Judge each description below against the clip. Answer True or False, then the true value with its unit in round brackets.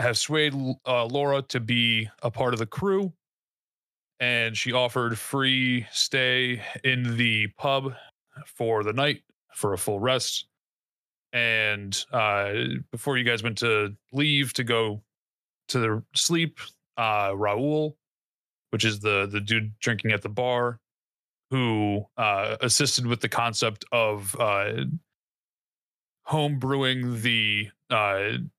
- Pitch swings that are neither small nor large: True (3.3 semitones)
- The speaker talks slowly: True (130 wpm)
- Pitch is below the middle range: True (120 Hz)